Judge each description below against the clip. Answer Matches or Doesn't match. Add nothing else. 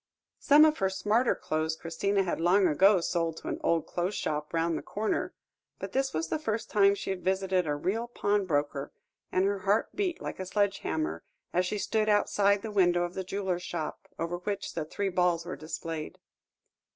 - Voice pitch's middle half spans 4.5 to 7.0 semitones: Doesn't match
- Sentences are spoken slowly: Doesn't match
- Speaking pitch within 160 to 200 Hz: Matches